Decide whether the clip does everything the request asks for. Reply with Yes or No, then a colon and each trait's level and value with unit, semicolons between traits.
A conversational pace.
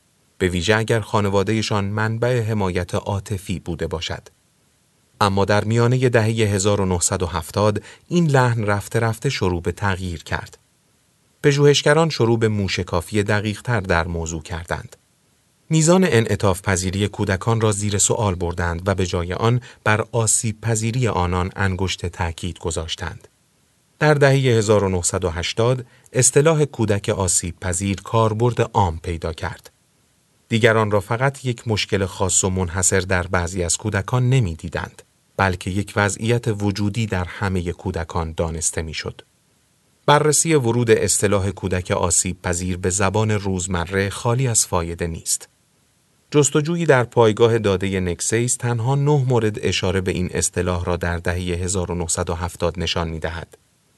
Yes: average, 130 wpm